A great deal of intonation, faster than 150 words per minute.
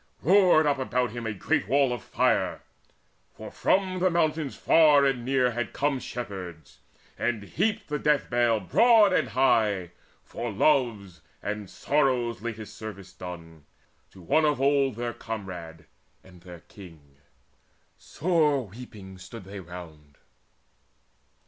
No: wide, 7.0 semitones; slow, 135 wpm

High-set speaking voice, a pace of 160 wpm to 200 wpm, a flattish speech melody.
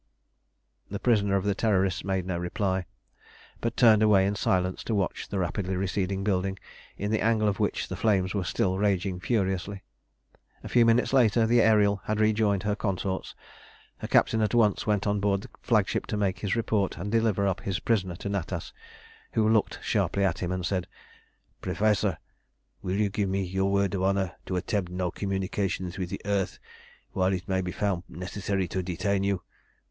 No: low, 100 Hz; average, 185 wpm; narrow, 2.0 semitones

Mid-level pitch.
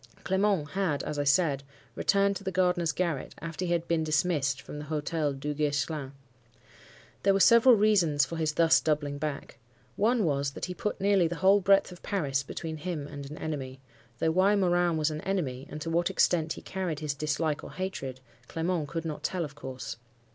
Yes: medium, 160 Hz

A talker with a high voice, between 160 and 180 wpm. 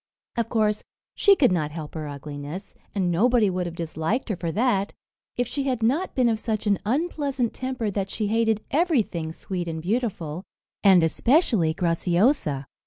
Yes: high, 205 Hz; average, 170 wpm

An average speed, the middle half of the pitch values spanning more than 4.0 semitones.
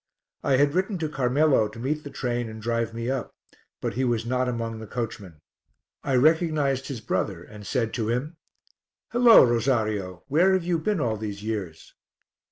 Yes: average, 175 wpm; average, 4.9 semitones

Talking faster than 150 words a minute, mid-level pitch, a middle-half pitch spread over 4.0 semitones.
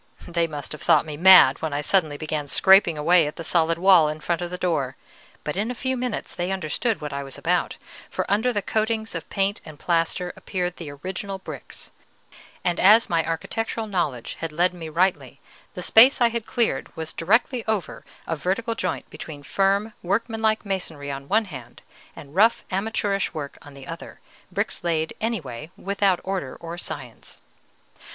Yes: average, 185 wpm; medium, 180 Hz; average, 4.8 semitones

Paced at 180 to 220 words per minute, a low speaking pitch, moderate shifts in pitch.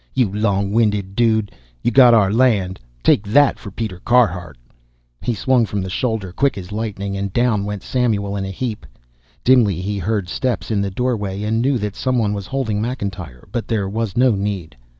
Yes: average, 190 wpm; low, 105 Hz; average, 3.3 semitones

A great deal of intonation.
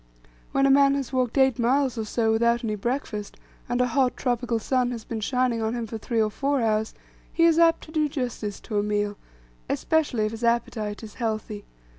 No: average, 3.4 semitones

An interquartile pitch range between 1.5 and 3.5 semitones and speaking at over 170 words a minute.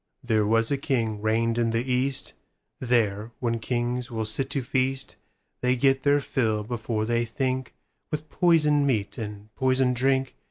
No: average, 2.9 semitones; average, 145 wpm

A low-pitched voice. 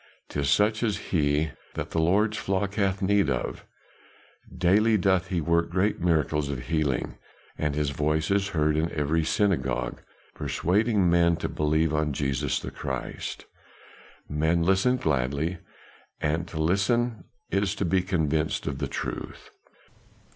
Yes: very low, 85 Hz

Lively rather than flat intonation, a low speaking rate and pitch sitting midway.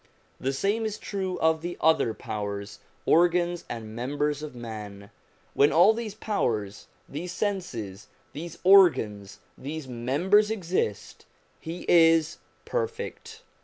Yes: wide, 8.3 semitones; slow, 120 wpm; medium, 160 Hz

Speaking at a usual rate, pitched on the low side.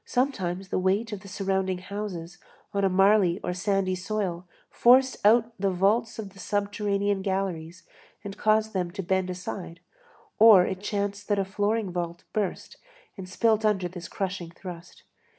No: average, 160 wpm; high, 195 Hz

